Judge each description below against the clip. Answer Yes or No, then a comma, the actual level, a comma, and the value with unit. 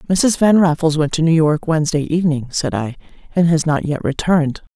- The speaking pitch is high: No, medium, 160 Hz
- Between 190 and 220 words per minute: Yes, average, 200 wpm